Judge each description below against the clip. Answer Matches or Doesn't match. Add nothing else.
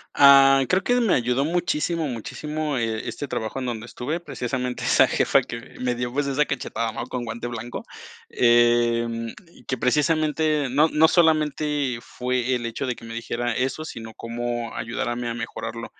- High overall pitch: Doesn't match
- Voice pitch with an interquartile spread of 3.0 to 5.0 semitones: Matches